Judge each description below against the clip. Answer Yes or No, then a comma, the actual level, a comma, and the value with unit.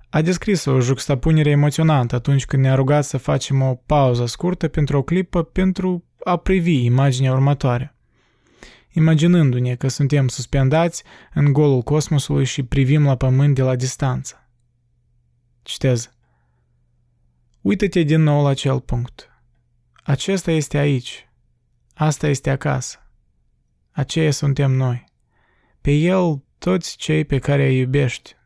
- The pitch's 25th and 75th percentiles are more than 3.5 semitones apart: No, average, 3.2 semitones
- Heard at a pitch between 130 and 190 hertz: Yes, medium, 140 Hz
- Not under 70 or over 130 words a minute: Yes, average, 125 wpm